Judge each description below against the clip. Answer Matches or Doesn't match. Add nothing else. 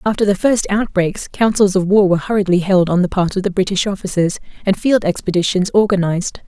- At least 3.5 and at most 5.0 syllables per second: Doesn't match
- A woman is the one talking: Matches